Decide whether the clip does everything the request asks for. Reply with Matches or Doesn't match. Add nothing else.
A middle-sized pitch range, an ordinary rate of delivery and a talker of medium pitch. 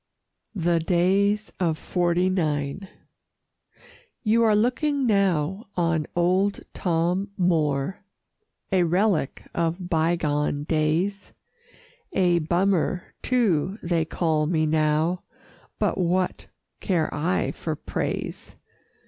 Doesn't match